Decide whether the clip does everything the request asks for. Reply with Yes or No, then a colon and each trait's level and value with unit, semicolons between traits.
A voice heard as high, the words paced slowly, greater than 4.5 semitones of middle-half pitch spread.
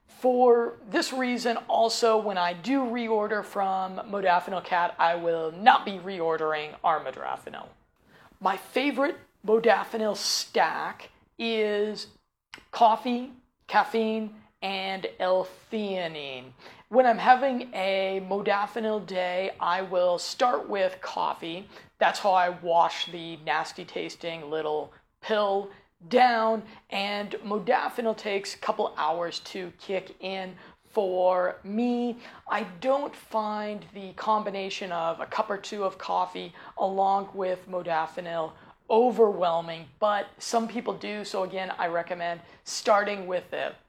No: high, 195 Hz; slow, 115 wpm; average, 3.8 semitones